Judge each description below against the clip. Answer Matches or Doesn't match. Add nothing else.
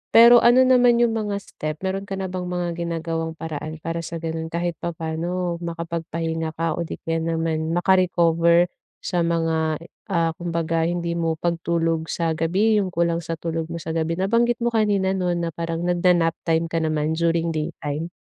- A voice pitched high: Doesn't match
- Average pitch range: Doesn't match